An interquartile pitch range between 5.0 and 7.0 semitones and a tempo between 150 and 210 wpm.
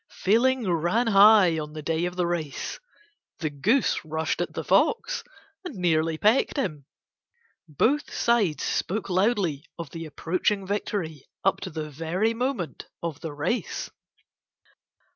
No: wide, 5.5 semitones; average, 140 wpm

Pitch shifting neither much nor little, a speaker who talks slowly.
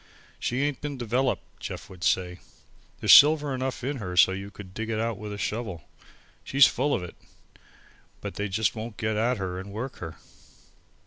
No: average, 5.0 semitones; average, 185 wpm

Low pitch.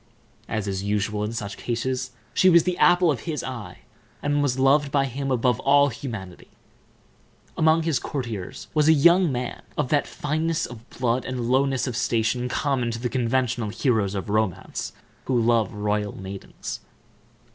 Yes: low, 125 Hz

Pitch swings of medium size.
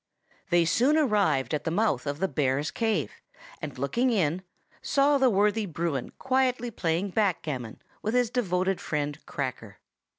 No: wide, 7.5 semitones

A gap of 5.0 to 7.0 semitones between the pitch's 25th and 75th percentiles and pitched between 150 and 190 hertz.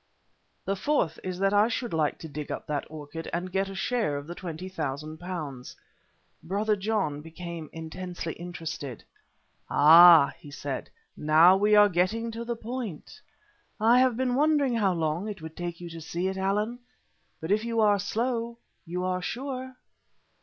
Yes: wide, 5.4 semitones; medium, 185 Hz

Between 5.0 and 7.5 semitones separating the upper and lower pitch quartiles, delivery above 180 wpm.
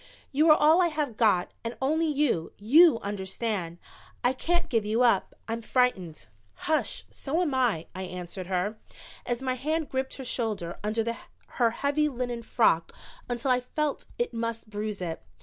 No: wide, 5.4 semitones; average, 165 wpm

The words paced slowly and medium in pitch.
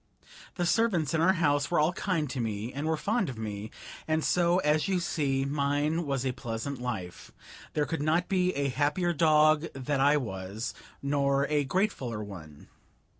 No: average, 175 wpm; medium, 145 Hz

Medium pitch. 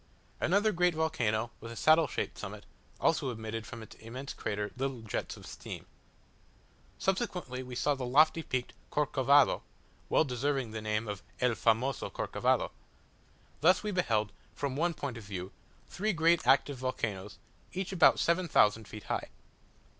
No: low, 130 Hz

